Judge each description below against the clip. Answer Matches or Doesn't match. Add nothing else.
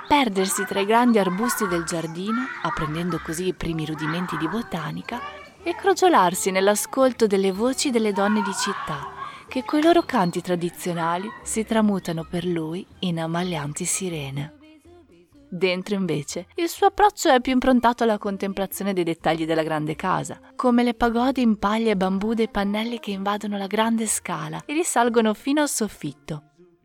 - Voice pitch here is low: Doesn't match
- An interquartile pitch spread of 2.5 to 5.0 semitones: Doesn't match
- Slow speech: Doesn't match